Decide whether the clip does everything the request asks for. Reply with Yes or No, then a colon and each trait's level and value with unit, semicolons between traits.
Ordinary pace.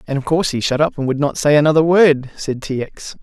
No: fast, 280 wpm